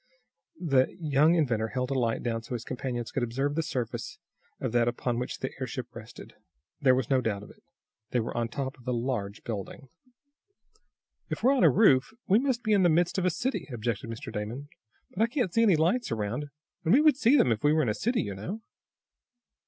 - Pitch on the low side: Yes, low, 130 Hz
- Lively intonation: Yes, wide, 6.8 semitones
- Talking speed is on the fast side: Yes, fast, 220 wpm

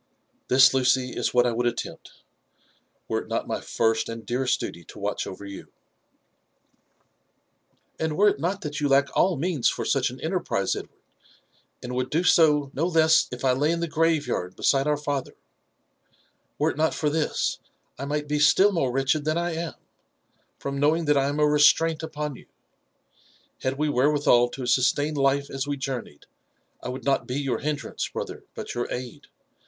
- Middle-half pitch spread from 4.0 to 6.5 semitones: No, average, 3.2 semitones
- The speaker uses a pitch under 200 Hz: Yes, medium, 140 Hz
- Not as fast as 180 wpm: No, average, 190 wpm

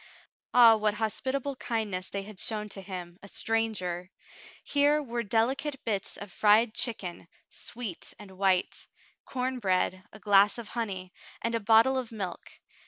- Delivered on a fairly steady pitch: No, average, 3.5 semitones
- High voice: Yes, high, 215 Hz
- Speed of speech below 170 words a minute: Yes, average, 150 wpm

